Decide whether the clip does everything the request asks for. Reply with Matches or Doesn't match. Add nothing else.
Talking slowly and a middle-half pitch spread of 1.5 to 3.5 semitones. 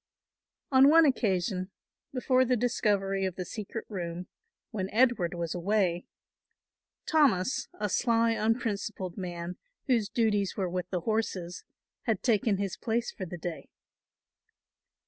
Doesn't match